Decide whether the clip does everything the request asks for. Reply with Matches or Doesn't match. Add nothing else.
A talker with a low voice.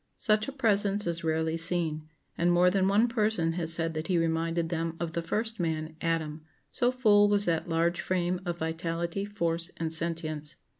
Doesn't match